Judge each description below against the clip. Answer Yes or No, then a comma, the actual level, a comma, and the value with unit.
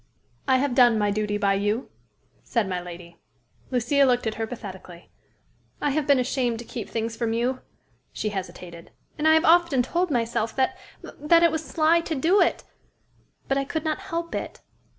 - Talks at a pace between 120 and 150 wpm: No, average, 185 wpm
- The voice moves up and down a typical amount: No, wide, 6.3 semitones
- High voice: Yes, high, 245 Hz